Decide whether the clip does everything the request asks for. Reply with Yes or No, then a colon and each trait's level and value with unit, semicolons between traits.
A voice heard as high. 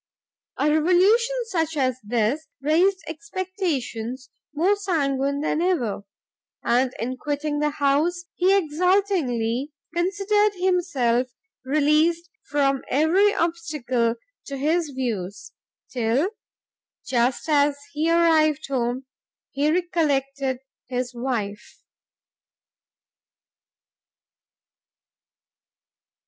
Yes: very high, 295 Hz